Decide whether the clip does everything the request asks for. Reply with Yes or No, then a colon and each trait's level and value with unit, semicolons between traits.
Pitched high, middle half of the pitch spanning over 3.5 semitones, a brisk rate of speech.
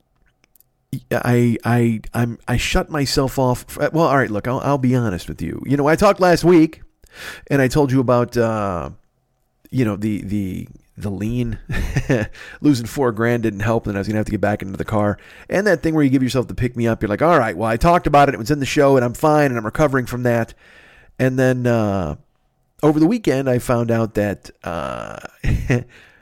No: low, 120 Hz; average, 4.3 semitones; fast, 215 wpm